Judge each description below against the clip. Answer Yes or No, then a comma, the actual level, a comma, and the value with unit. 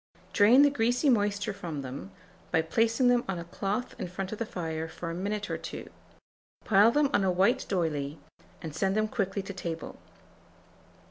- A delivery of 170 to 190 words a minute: Yes, average, 185 wpm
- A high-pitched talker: Yes, high, 195 Hz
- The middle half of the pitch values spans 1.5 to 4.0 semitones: No, average, 4.9 semitones